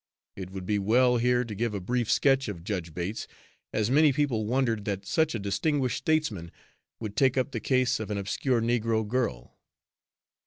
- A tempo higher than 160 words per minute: Yes, average, 185 wpm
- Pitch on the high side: No, low, 115 Hz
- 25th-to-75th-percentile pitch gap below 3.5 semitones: No, average, 4.1 semitones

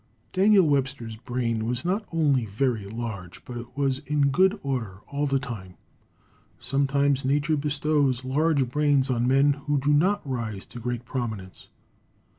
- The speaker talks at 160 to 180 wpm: No, average, 150 wpm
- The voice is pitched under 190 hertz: Yes, low, 135 Hz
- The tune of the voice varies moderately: Yes, average, 3.5 semitones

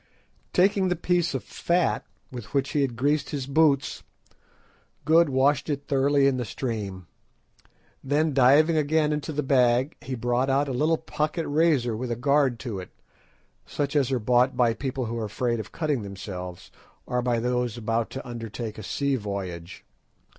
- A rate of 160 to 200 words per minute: Yes, average, 170 wpm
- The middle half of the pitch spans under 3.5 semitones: No, average, 3.8 semitones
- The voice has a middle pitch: No, low, 130 Hz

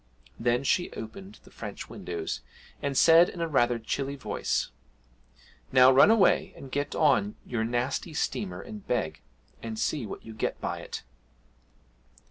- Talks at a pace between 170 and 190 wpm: No, average, 150 wpm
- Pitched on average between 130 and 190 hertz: Yes, low, 135 Hz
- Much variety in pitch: Yes, wide, 5.9 semitones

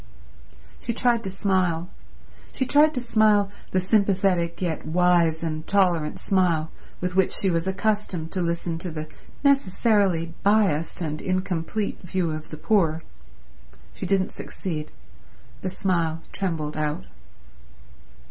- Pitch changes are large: No, average, 3.3 semitones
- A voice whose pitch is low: No, medium, 180 Hz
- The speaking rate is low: Yes, slow, 130 wpm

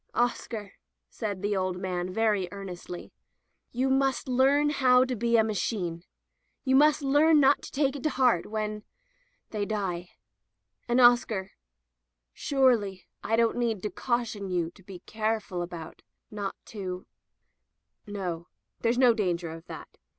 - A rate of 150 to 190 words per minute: Yes, average, 160 wpm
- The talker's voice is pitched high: Yes, high, 215 Hz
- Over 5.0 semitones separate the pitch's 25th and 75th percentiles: Yes, wide, 5.4 semitones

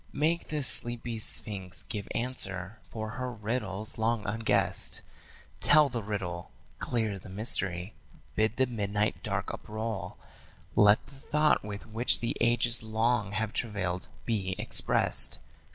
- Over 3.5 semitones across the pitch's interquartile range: No, average, 2.8 semitones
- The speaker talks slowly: Yes, slow, 130 wpm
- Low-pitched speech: Yes, low, 110 Hz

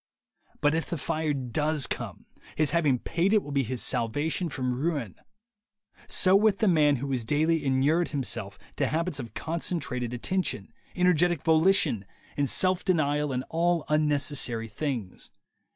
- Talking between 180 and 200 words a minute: No, average, 145 wpm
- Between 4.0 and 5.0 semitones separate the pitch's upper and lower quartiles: Yes, average, 4.3 semitones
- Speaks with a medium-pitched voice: Yes, medium, 150 Hz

